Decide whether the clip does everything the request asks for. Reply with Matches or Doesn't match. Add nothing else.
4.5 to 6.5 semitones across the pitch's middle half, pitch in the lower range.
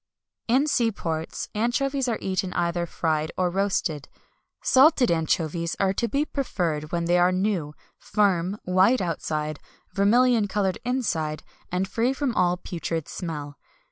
Doesn't match